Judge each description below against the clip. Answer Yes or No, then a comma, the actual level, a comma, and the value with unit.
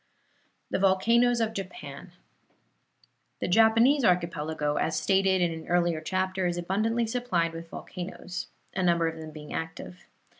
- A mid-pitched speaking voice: Yes, medium, 180 Hz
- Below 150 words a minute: Yes, average, 140 wpm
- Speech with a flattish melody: No, average, 4.6 semitones